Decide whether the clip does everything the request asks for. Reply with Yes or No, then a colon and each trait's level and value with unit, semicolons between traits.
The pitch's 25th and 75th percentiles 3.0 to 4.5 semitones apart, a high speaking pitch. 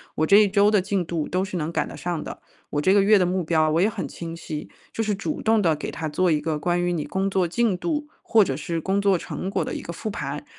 No: average, 3.7 semitones; medium, 180 Hz